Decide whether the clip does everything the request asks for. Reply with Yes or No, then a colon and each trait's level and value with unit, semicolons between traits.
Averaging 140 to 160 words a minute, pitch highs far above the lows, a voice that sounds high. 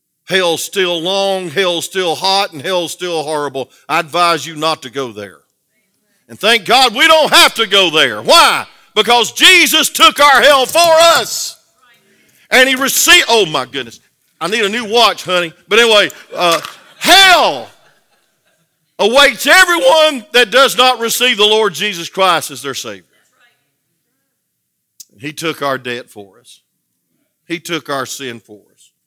Yes: average, 155 wpm; wide, 8.4 semitones; high, 195 Hz